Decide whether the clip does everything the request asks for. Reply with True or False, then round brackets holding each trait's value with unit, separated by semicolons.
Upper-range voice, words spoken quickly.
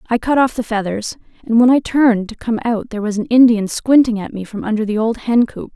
True (225 Hz; 260 wpm)